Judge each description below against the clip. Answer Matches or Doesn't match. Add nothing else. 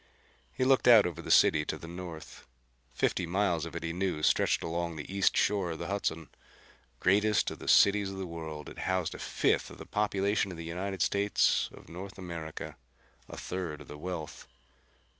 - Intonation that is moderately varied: Matches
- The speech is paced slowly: Doesn't match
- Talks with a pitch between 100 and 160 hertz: Doesn't match